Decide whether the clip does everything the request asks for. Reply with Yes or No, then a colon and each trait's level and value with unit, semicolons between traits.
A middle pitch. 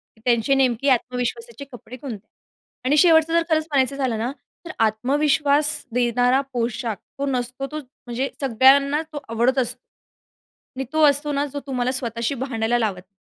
No: very high, 260 Hz